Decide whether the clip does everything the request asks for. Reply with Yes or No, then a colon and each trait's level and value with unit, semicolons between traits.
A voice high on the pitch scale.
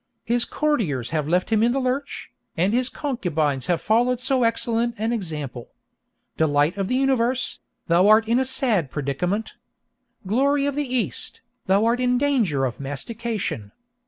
Yes: high, 225 Hz